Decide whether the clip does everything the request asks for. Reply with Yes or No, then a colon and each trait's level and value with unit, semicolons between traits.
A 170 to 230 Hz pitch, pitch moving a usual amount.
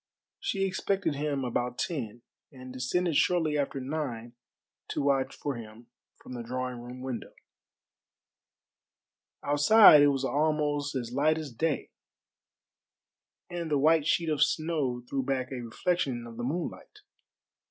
No: medium, 140 Hz; average, 3.8 semitones